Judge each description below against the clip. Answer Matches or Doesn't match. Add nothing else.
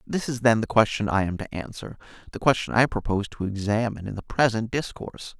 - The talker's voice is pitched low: Matches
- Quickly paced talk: Matches